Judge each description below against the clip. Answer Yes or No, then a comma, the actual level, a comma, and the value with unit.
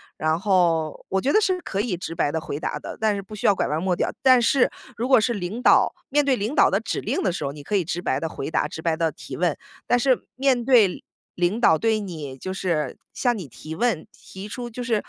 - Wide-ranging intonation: Yes, wide, 6.7 semitones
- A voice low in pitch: No, high, 195 Hz